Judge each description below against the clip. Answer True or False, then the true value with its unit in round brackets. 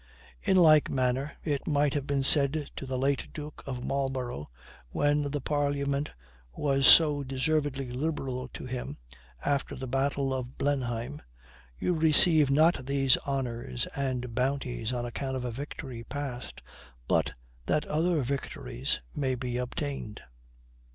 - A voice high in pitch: False (135 Hz)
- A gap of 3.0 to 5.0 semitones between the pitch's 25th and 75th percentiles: False (2.4 semitones)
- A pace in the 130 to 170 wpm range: True (140 wpm)